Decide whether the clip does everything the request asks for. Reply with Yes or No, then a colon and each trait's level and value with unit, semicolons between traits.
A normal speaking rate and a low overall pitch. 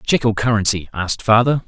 Yes: average, 180 wpm; low, 110 Hz